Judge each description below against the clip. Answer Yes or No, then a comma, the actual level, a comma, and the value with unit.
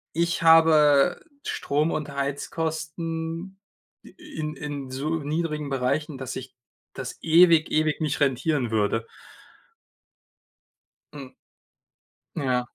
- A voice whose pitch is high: No, medium, 150 Hz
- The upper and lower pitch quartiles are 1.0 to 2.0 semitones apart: No, average, 2.8 semitones